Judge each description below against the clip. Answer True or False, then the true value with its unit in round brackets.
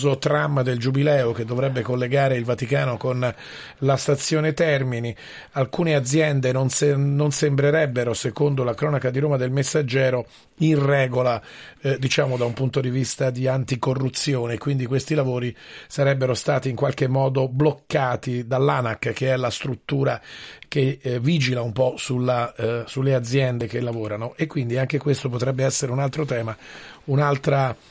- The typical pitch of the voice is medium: False (130 Hz)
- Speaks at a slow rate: False (155 wpm)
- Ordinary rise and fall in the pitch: False (2.2 semitones)